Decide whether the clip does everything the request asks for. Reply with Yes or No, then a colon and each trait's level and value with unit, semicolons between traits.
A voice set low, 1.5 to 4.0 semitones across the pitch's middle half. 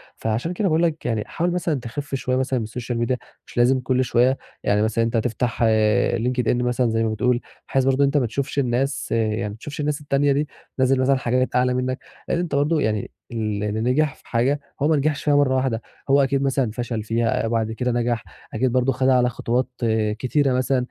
Yes: low, 125 Hz; average, 2.9 semitones